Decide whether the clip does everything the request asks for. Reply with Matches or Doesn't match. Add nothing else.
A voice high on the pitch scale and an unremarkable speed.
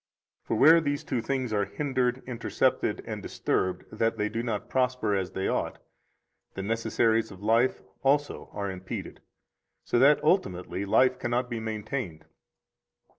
Doesn't match